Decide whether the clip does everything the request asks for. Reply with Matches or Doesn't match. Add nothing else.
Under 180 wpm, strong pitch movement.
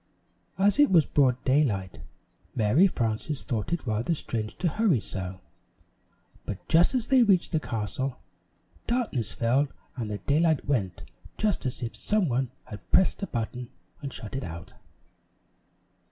Matches